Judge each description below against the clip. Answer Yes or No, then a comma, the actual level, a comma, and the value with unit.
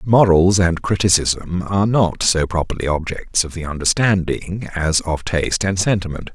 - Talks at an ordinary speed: Yes, average, 150 wpm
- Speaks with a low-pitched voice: Yes, very low, 90 Hz